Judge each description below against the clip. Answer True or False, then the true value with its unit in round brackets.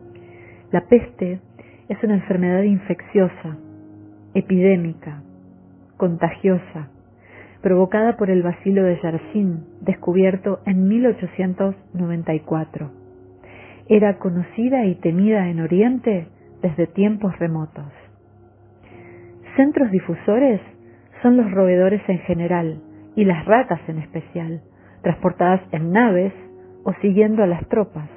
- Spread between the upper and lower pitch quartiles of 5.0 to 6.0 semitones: True (5.4 semitones)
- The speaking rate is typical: False (100 wpm)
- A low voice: False (175 Hz)